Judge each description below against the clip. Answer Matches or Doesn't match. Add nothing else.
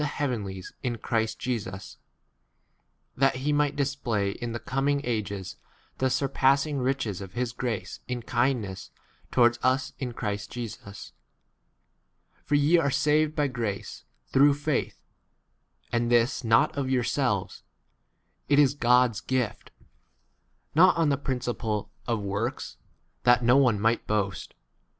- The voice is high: Doesn't match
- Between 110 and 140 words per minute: Matches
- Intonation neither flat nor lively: Matches